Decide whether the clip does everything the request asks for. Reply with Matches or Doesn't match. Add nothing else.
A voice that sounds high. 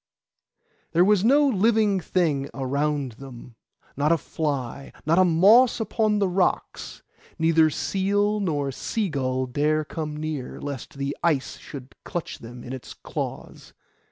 Doesn't match